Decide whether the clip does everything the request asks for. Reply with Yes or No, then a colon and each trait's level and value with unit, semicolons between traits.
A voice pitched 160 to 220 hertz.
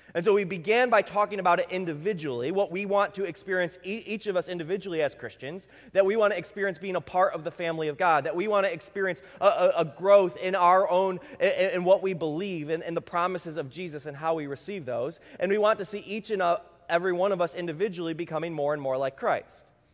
Yes: medium, 185 Hz